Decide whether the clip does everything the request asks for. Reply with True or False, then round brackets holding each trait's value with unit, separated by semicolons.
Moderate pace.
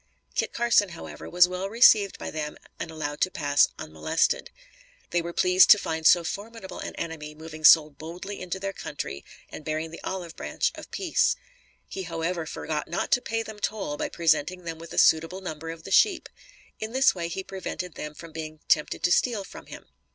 True (195 wpm)